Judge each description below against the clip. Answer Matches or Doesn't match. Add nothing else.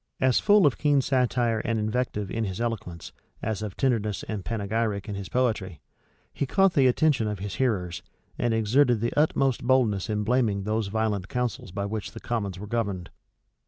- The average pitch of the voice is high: Doesn't match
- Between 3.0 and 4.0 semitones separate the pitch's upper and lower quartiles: Matches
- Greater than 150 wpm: Matches